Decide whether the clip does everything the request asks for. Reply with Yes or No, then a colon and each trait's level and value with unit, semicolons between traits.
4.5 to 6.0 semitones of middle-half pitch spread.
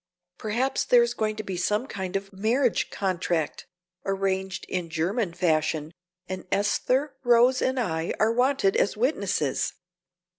Yes: average, 5.1 semitones